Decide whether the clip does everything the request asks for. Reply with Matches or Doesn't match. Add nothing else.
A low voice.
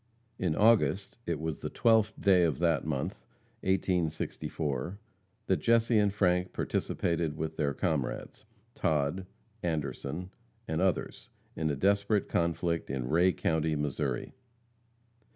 Matches